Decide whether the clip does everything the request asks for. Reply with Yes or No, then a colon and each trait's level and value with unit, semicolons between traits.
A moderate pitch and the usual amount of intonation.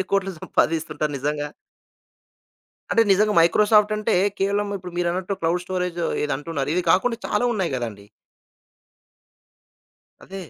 Yes: medium, 180 Hz; average, 4.0 semitones